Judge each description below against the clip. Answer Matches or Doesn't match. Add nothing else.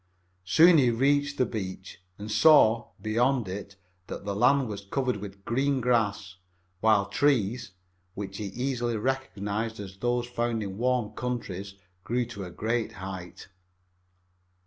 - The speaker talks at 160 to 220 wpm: Doesn't match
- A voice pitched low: Matches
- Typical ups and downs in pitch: Matches